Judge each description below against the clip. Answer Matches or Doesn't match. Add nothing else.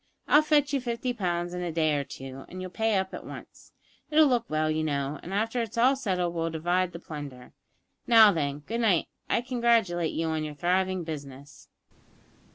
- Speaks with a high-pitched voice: Doesn't match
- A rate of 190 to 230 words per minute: Matches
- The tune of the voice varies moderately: Doesn't match